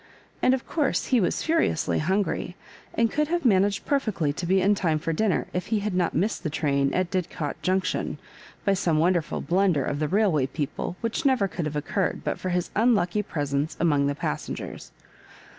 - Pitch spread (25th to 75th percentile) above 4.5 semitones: Yes, average, 5.1 semitones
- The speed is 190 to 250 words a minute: Yes, average, 195 wpm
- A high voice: No, medium, 180 Hz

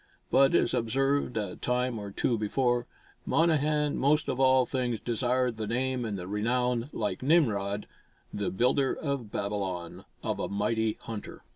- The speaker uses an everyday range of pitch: Yes, average, 4.0 semitones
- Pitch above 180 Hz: No, low, 120 Hz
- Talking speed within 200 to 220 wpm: No, average, 150 wpm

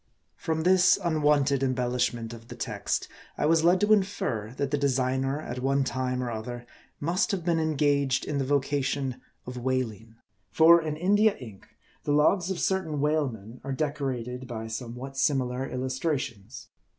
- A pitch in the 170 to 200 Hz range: No, low, 135 Hz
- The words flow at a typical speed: Yes, average, 155 wpm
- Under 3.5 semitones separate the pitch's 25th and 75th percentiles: No, average, 3.8 semitones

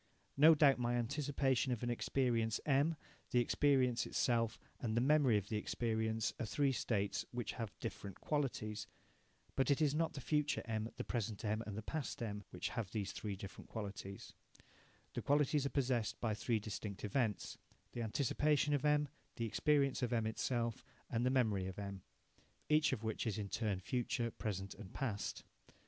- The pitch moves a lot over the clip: No, average, 4.3 semitones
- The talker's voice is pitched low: Yes, low, 115 Hz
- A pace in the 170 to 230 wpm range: Yes, average, 175 wpm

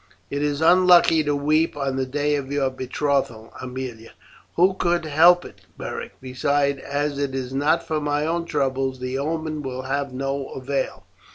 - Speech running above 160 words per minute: Yes, average, 170 wpm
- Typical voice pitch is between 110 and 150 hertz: Yes, medium, 140 Hz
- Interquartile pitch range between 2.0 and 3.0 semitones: Yes, narrow, 2.6 semitones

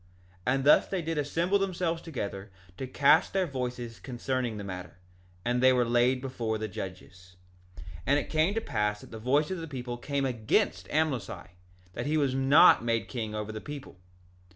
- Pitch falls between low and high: No, low, 130 Hz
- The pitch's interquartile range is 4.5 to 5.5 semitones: Yes, average, 5.2 semitones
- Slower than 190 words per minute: No, average, 195 wpm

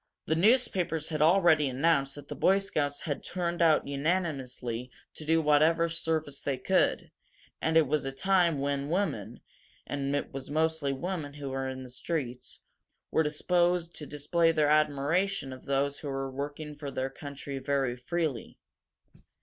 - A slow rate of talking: No, average, 160 wpm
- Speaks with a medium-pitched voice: Yes, medium, 150 Hz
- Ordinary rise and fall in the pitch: Yes, average, 3.2 semitones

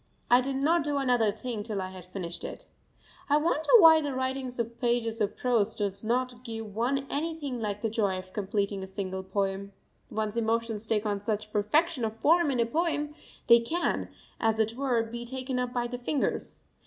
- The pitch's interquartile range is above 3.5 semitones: Yes, average, 4.2 semitones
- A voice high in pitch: Yes, high, 235 Hz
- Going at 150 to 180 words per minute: No, average, 195 wpm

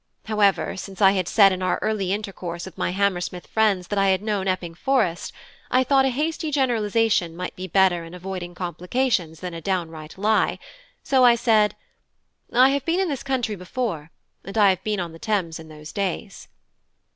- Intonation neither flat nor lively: Yes, average, 4.1 semitones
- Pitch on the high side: Yes, high, 195 Hz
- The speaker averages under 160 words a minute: No, average, 190 wpm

